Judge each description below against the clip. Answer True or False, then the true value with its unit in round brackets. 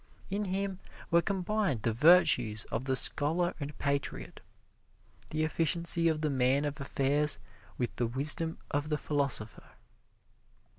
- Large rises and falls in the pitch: False (3.8 semitones)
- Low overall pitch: False (150 Hz)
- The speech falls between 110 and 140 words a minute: True (135 wpm)